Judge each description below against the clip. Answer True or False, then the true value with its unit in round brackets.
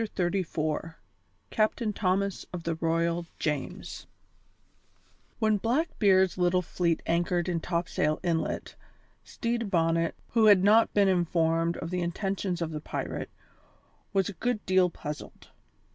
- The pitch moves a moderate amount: True (3.1 semitones)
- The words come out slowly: True (130 wpm)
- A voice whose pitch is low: False (180 Hz)